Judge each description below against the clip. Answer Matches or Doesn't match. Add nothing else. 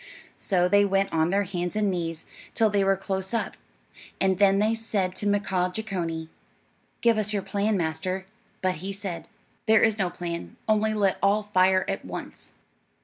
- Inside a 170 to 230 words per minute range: Matches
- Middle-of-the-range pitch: Doesn't match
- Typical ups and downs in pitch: Doesn't match